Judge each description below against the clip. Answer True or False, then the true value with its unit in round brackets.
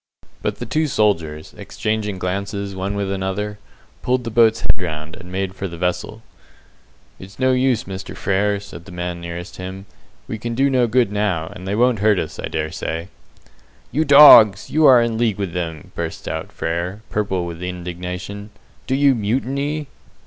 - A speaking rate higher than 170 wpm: True (180 wpm)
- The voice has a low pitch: True (100 Hz)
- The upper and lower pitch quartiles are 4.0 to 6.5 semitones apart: True (4.4 semitones)